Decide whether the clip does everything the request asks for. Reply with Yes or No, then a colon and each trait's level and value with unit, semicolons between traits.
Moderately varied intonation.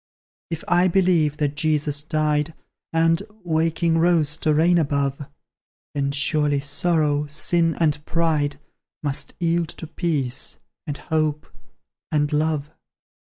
No: narrow, 2.1 semitones